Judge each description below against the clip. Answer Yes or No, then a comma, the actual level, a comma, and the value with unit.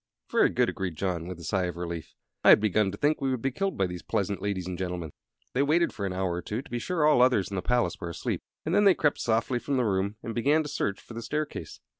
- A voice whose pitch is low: Yes, low, 105 Hz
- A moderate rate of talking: No, fast, 280 wpm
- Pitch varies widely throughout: Yes, wide, 6.6 semitones